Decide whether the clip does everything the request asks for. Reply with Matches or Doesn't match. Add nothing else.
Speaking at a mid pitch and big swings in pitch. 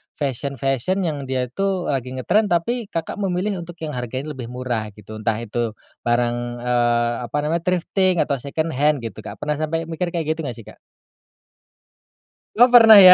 Matches